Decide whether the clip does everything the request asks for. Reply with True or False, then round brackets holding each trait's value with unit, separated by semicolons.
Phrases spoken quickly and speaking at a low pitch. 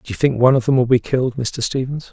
True (310 wpm; 125 Hz)